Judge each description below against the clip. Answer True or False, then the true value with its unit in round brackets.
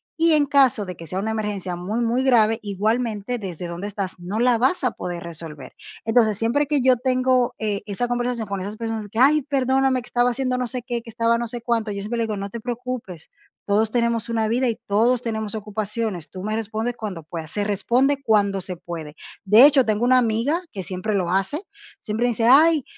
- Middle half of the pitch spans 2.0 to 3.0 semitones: False (3.7 semitones)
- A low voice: False (225 Hz)